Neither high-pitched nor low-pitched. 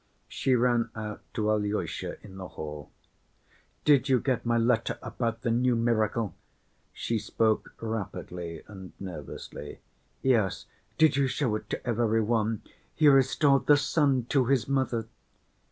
No: low, 115 Hz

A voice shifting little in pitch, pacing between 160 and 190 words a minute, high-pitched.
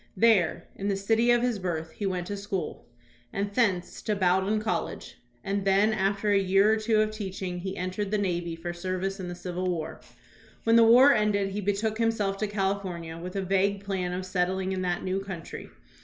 No: narrow, 2.3 semitones; fast, 205 wpm; high, 195 Hz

